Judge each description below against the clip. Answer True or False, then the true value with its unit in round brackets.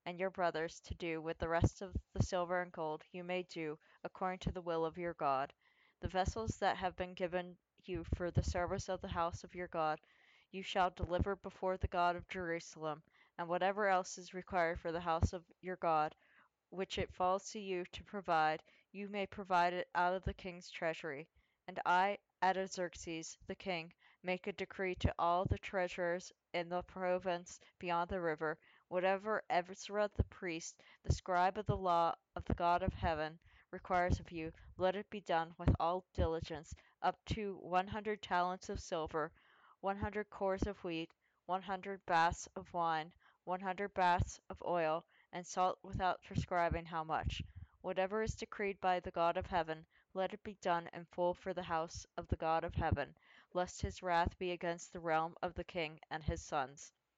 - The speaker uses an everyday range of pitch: False (2.0 semitones)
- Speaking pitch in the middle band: True (180 Hz)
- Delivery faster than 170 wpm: True (190 wpm)